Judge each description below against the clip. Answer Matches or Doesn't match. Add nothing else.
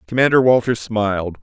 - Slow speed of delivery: Matches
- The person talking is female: Doesn't match